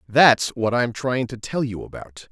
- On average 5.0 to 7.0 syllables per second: No, 4.3 syllables/s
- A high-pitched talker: No, low, 120 Hz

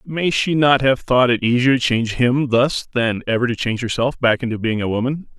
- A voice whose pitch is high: No, low, 125 Hz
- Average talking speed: No, fast, 235 wpm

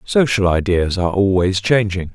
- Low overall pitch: Yes, low, 100 Hz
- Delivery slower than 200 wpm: Yes, average, 140 wpm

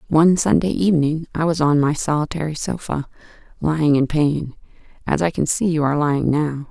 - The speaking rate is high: No, average, 160 wpm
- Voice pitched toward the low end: No, medium, 155 Hz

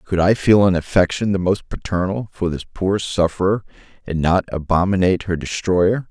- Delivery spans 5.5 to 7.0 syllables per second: No, 5.1 syllables/s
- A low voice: Yes, very low, 90 Hz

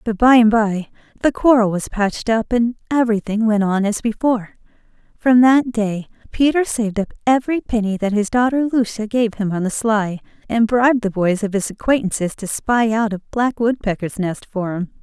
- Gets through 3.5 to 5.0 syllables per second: No, 5.3 syllables/s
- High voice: Yes, high, 220 Hz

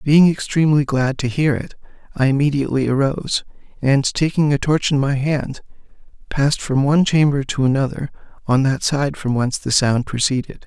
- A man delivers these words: Yes, male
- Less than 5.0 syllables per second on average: No, 5.4 syllables/s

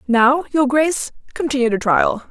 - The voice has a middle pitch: No, very high, 265 Hz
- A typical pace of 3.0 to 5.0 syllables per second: Yes, 4.8 syllables/s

